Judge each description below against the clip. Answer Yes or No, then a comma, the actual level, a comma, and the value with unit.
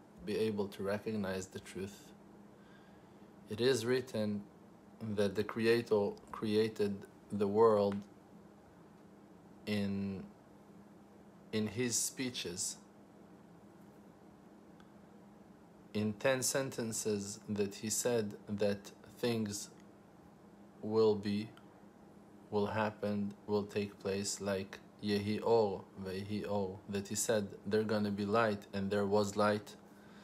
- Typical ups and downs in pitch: No, narrow, 1.4 semitones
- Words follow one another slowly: Yes, slow, 100 wpm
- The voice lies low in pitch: Yes, low, 105 Hz